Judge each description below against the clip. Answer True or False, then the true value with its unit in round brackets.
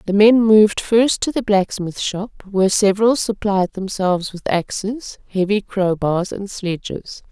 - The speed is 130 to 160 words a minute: True (155 wpm)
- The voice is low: False (200 Hz)